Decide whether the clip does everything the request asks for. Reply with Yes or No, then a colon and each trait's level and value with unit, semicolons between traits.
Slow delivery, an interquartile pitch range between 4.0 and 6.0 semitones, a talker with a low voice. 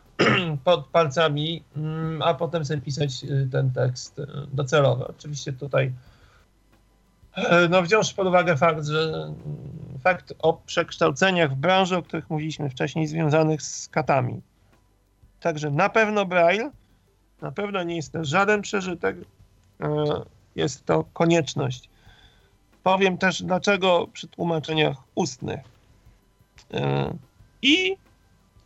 No: slow, 105 wpm; average, 5.3 semitones; medium, 155 Hz